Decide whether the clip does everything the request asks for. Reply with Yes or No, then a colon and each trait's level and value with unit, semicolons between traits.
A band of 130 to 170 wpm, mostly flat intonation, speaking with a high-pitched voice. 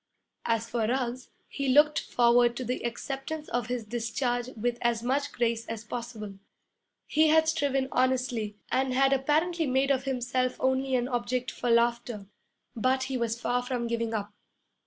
Yes: average, 160 wpm; narrow, 2.2 semitones; high, 245 Hz